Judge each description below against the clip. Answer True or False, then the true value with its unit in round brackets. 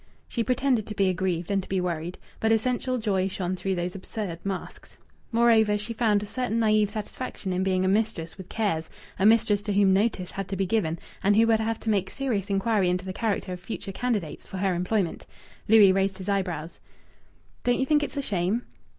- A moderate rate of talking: False (210 wpm)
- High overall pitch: True (200 Hz)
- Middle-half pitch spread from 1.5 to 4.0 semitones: True (3.1 semitones)